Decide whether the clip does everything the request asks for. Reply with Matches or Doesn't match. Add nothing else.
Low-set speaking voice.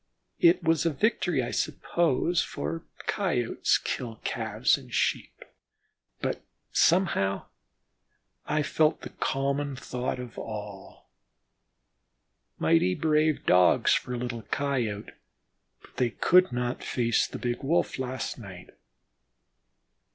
Matches